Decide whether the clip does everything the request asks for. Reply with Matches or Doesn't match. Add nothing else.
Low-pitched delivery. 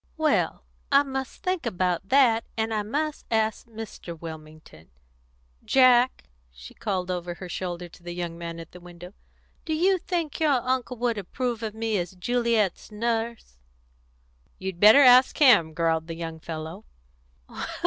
Doesn't match